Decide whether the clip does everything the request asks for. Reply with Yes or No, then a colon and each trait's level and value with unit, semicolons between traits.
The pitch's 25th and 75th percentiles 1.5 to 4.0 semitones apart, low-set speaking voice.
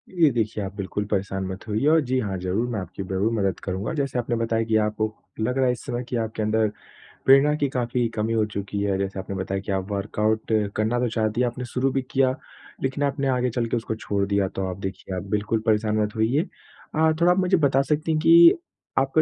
No: average, 4.5 semitones; low, 110 Hz